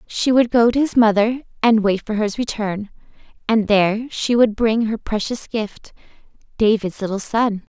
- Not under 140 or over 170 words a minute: Yes, average, 165 wpm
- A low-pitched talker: No, high, 220 Hz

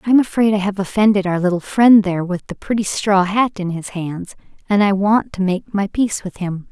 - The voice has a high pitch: Yes, high, 195 Hz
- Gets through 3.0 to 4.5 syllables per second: No, 5.5 syllables/s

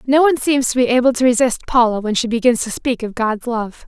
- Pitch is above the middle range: Yes, high, 240 Hz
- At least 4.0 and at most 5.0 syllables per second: No, 6.0 syllables/s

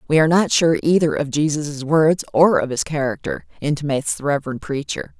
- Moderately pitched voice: Yes, medium, 150 Hz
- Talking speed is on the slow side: No, average, 185 wpm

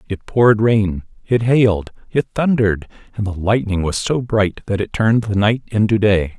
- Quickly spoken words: No, average, 190 wpm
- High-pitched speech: No, low, 105 Hz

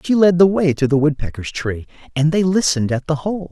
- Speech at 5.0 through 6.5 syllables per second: Yes, 5.8 syllables/s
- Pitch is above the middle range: No, medium, 155 Hz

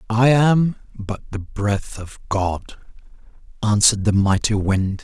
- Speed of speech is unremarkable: No, slow, 130 wpm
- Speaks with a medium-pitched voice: No, low, 105 Hz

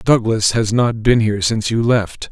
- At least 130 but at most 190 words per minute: No, fast, 205 wpm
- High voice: No, low, 110 Hz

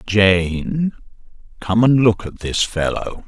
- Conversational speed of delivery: No, slow, 130 wpm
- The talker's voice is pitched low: Yes, low, 105 Hz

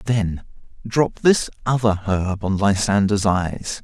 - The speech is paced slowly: Yes, slow, 125 wpm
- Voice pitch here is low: Yes, low, 105 Hz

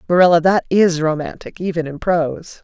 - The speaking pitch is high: No, medium, 170 Hz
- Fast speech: No, average, 160 wpm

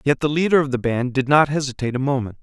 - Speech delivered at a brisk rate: Yes, fast, 270 wpm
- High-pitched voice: No, low, 135 Hz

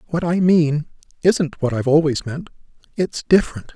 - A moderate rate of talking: Yes, average, 160 wpm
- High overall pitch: No, medium, 160 Hz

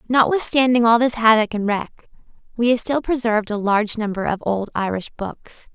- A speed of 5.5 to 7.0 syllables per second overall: No, 5.2 syllables/s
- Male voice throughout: No, female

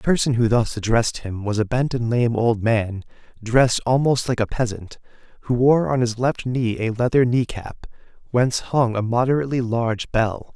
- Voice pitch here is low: Yes, low, 120 Hz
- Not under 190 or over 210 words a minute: Yes, average, 195 wpm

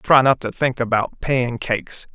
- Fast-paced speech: No, average, 170 wpm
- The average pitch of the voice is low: Yes, low, 125 Hz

